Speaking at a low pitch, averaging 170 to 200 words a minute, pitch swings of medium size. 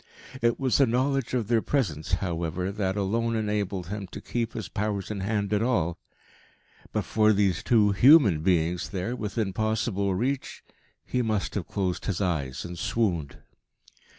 No: low, 105 Hz; average, 160 wpm; average, 3.9 semitones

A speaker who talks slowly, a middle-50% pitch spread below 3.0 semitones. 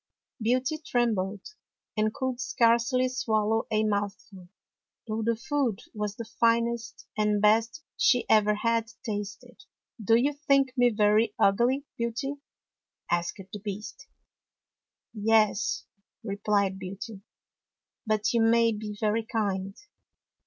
Yes: slow, 125 wpm; narrow, 2.4 semitones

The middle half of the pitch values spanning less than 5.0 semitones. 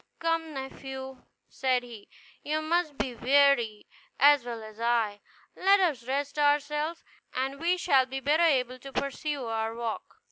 Yes: average, 3.6 semitones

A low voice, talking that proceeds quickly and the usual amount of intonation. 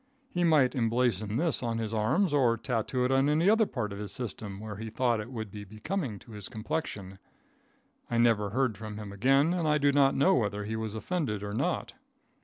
Yes: low, 115 Hz; fast, 210 wpm; average, 4.6 semitones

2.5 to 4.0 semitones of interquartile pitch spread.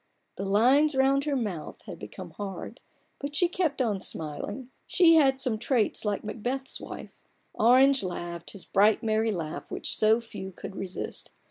No: average, 5.3 semitones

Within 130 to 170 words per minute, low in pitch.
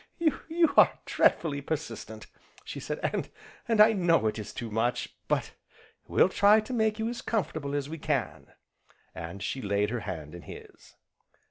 No: average, 160 wpm; medium, 145 Hz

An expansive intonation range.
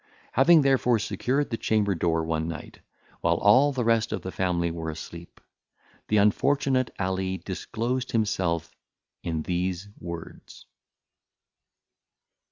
Yes: wide, 6.2 semitones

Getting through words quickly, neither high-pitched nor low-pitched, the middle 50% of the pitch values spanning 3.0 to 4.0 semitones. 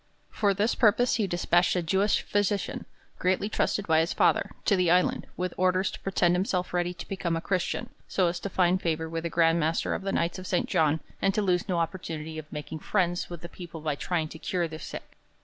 No: fast, 225 wpm; medium, 175 Hz; narrow, 2.5 semitones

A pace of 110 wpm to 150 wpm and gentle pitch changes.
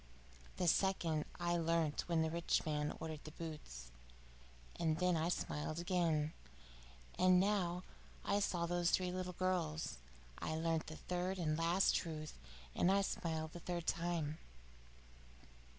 Yes: average, 140 wpm; narrow, 2.2 semitones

